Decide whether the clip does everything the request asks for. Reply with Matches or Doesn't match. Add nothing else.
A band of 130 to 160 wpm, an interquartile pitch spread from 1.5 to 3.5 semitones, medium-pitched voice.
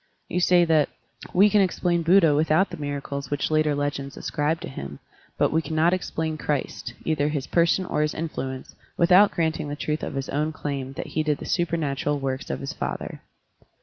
Doesn't match